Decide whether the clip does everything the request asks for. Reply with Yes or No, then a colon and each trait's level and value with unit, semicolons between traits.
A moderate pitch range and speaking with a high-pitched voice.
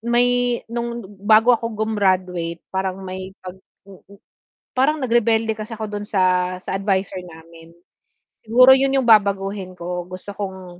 Yes: average, 3.8 semitones; high, 200 Hz